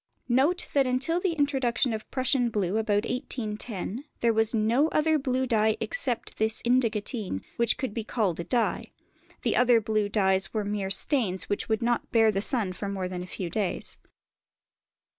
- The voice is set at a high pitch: Yes, high, 225 Hz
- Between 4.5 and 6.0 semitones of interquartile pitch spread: No, average, 3.7 semitones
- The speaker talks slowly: No, average, 175 wpm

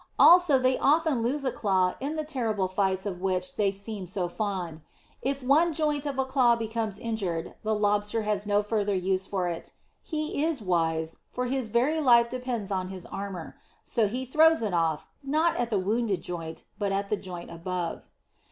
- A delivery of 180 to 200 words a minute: Yes, average, 190 wpm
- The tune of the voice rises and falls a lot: Yes, wide, 5.7 semitones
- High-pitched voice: Yes, high, 210 Hz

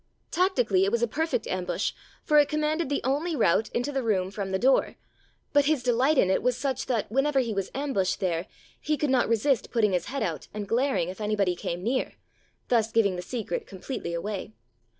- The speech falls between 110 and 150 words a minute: No, fast, 205 wpm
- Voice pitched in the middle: No, high, 230 Hz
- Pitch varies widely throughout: Yes, wide, 6.1 semitones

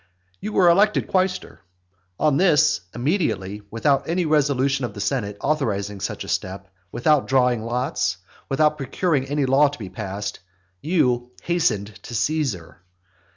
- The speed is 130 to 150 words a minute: Yes, average, 140 wpm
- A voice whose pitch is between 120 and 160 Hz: Yes, low, 135 Hz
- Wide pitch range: Yes, wide, 6.6 semitones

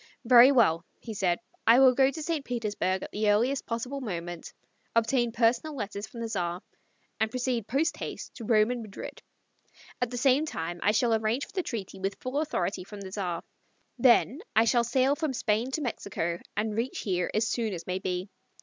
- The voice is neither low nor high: No, high, 230 Hz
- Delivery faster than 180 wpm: Yes, average, 195 wpm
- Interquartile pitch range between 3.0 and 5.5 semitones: Yes, average, 4.3 semitones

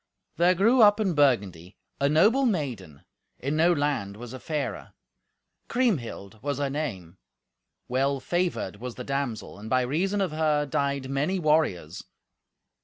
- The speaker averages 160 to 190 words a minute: No, average, 145 wpm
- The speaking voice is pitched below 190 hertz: Yes, medium, 140 Hz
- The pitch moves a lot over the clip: Yes, wide, 5.7 semitones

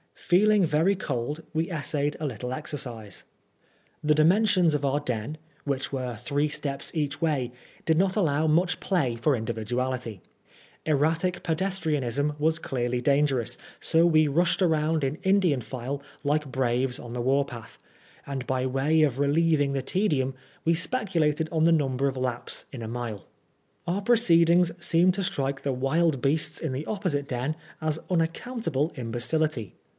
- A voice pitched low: No, medium, 150 Hz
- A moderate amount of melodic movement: Yes, average, 4.1 semitones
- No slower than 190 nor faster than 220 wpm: No, average, 155 wpm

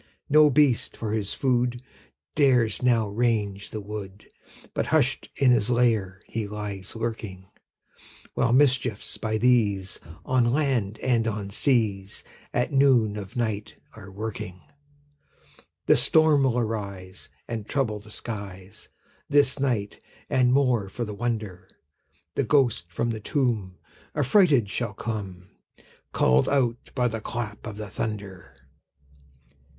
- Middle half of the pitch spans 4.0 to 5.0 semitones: No, average, 3.5 semitones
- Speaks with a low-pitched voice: Yes, low, 110 Hz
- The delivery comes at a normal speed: No, slow, 130 wpm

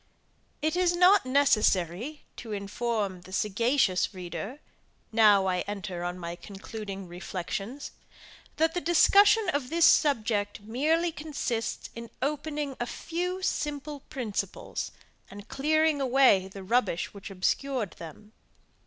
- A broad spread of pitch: Yes, wide, 7.2 semitones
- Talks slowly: Yes, slow, 120 wpm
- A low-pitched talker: No, high, 235 Hz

